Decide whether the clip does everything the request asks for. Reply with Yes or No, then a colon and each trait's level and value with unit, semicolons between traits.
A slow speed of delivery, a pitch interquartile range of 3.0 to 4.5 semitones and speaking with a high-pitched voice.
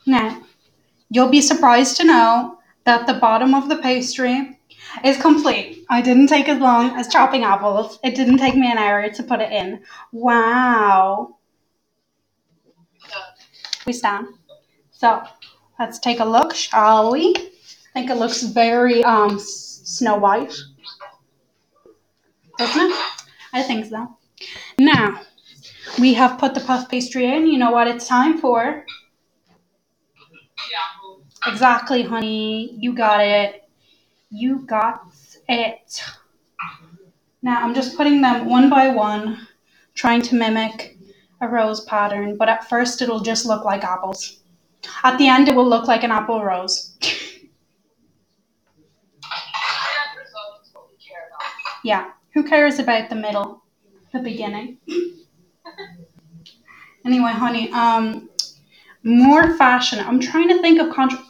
Yes: slow, 125 wpm; average, 3.4 semitones; high, 240 Hz